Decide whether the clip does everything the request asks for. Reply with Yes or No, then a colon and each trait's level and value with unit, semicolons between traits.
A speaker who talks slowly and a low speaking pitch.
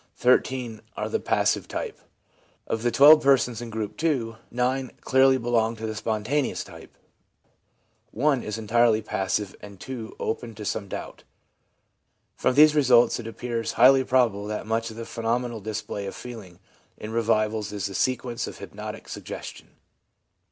No: average, 160 wpm; low, 115 Hz